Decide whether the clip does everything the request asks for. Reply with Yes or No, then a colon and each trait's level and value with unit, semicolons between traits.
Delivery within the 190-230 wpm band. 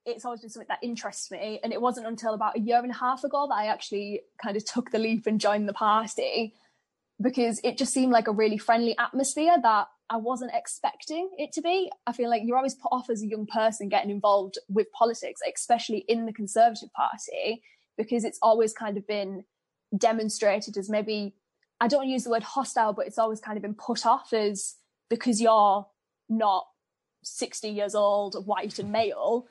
Yes: average, 200 wpm